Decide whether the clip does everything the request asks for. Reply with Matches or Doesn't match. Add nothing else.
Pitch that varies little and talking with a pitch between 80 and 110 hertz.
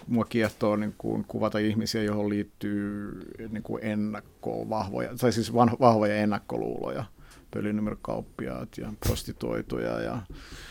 Matches